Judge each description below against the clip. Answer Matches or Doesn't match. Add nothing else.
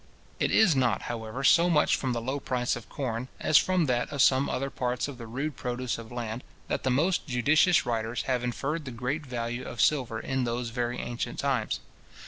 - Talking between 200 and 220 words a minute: Matches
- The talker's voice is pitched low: Matches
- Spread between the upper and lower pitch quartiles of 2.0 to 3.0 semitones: Matches